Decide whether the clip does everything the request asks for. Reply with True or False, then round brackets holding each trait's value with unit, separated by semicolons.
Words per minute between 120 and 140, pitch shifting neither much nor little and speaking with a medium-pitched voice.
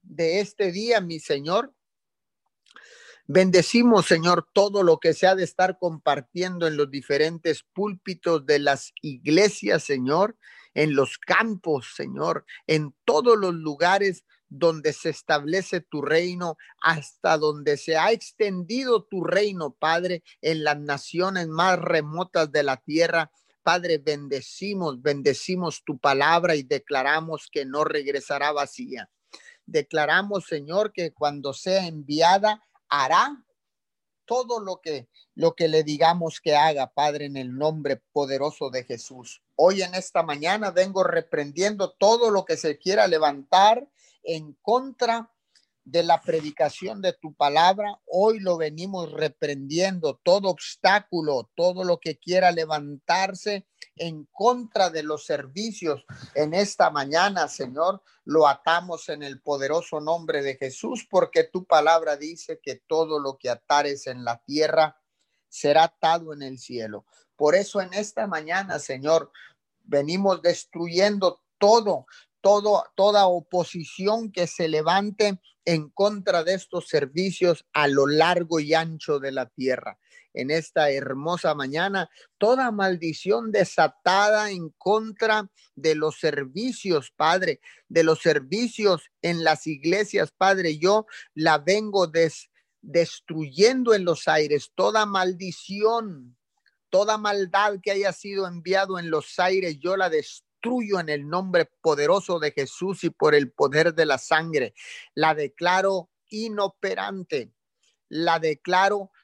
True (130 wpm; 4.2 semitones; 170 Hz)